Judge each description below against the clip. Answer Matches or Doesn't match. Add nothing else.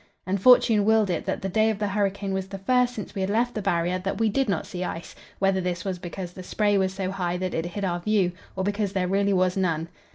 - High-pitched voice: Matches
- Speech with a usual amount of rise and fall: Doesn't match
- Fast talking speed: Matches